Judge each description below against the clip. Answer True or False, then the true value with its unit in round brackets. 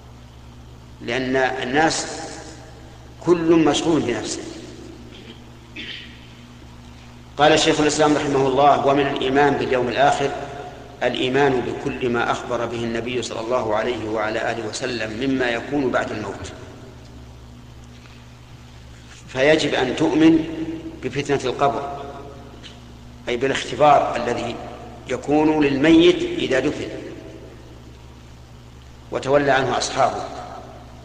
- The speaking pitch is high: False (115 Hz)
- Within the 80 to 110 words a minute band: True (85 wpm)